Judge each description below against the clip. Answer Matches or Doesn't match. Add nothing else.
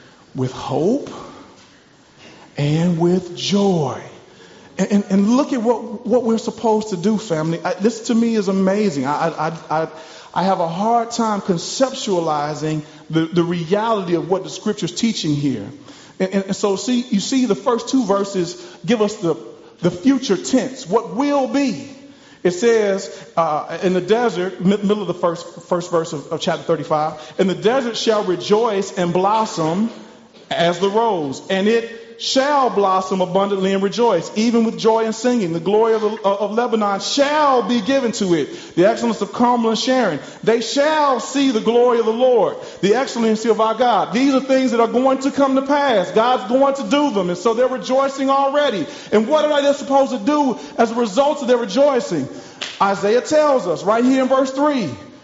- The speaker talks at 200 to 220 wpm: Doesn't match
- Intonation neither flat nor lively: Doesn't match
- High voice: Matches